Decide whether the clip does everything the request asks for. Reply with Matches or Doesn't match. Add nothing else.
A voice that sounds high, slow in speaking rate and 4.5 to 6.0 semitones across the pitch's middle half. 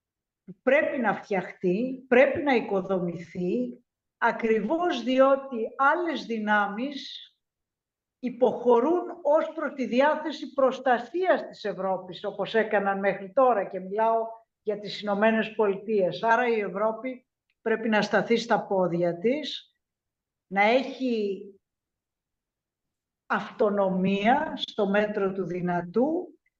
Matches